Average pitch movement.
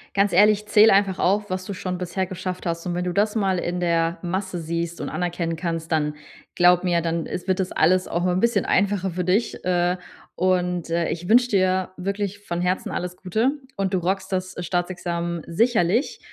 No: narrow, 2.0 semitones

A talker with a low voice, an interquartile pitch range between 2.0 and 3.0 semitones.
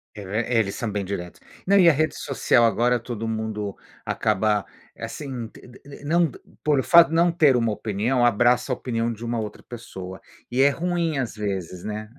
No: low, 120 Hz; average, 4.7 semitones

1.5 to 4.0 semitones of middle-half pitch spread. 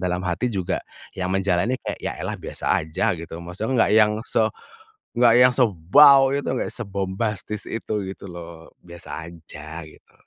No: average, 4.9 semitones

